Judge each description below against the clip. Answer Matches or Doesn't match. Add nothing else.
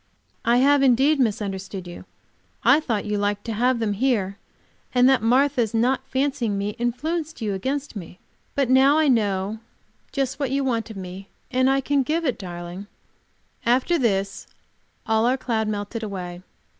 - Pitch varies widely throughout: Doesn't match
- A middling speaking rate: Matches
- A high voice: Matches